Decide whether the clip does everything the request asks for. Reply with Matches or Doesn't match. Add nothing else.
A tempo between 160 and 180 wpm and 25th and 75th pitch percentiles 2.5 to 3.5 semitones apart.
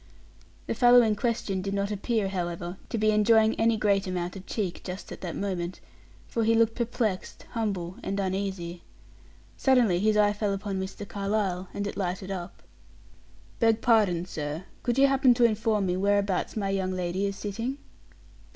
Matches